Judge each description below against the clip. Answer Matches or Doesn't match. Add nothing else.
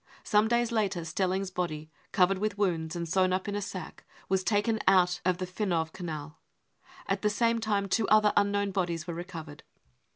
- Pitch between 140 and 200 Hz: Matches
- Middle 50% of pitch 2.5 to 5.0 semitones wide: Matches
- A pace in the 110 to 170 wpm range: Doesn't match